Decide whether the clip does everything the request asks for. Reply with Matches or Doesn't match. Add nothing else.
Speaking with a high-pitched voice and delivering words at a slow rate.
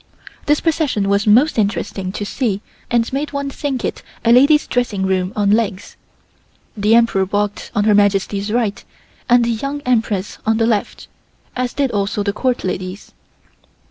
Doesn't match